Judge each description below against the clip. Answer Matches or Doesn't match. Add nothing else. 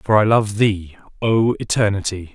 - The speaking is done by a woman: Doesn't match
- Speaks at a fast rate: Doesn't match